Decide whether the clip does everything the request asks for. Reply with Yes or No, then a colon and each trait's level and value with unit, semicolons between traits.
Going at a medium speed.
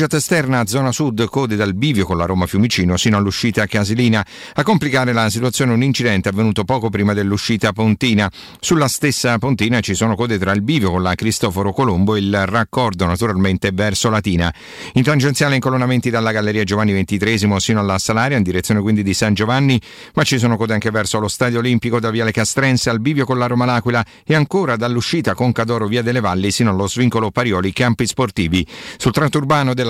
No: fast, 185 wpm